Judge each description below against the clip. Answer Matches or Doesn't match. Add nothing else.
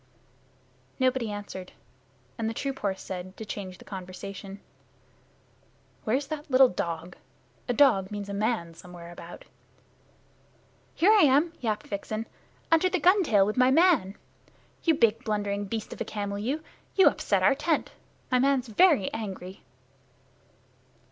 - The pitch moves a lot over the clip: Matches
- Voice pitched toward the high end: Matches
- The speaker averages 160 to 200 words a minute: Doesn't match